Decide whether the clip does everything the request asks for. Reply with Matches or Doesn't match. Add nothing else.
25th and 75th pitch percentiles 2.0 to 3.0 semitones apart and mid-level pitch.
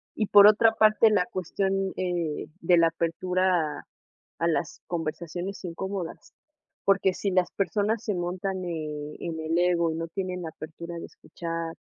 Matches